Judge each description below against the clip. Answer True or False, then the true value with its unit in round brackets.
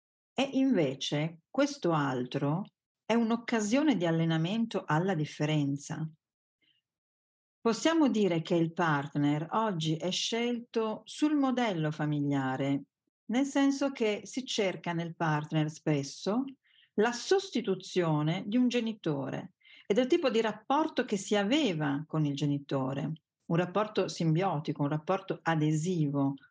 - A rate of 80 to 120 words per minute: True (115 wpm)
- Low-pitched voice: False (175 Hz)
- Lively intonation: True (7.3 semitones)